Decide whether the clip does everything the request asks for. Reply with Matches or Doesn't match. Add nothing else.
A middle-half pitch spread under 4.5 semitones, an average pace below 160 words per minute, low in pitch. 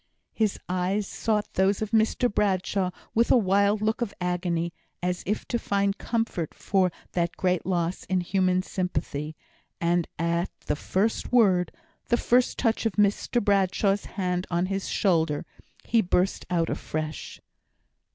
Doesn't match